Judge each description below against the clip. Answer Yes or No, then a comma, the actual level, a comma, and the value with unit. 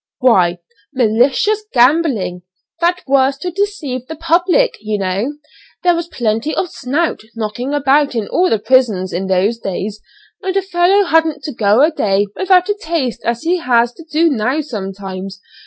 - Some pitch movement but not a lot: No, wide, 7.8 semitones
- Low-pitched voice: No, very high, 265 Hz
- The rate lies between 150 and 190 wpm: Yes, average, 165 wpm